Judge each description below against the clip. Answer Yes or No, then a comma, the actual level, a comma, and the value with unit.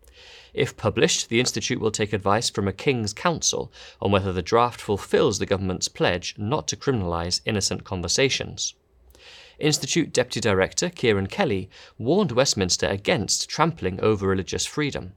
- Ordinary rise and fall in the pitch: Yes, average, 4.2 semitones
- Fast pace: No, average, 140 wpm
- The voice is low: Yes, low, 105 Hz